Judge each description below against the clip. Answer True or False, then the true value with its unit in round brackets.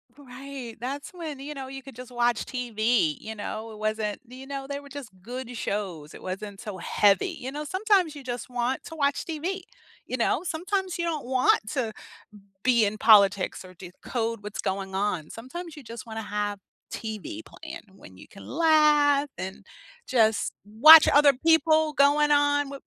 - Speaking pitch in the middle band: False (255 Hz)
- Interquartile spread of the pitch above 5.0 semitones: True (5.5 semitones)